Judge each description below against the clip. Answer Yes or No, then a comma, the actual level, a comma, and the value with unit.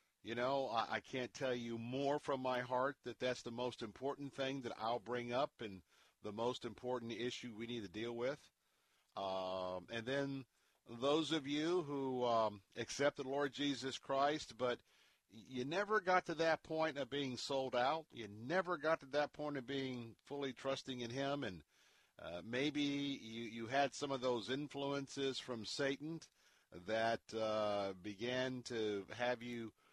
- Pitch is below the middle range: Yes, low, 125 Hz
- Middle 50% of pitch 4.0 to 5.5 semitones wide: No, average, 3.3 semitones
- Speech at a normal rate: Yes, average, 170 wpm